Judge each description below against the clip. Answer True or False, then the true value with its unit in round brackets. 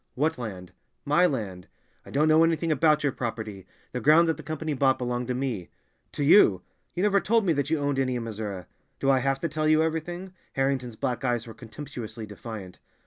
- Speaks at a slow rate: False (205 wpm)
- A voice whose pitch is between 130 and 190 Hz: True (135 Hz)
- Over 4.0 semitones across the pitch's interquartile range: True (5.4 semitones)